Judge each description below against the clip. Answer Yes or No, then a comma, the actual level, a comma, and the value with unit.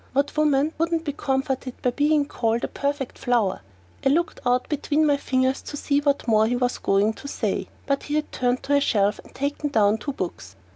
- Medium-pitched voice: No, very high, 270 Hz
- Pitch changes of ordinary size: Yes, average, 3.0 semitones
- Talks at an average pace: No, fast, 210 wpm